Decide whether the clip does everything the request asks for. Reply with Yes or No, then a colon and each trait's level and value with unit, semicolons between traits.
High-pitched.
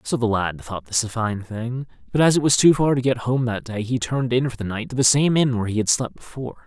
No: low, 120 Hz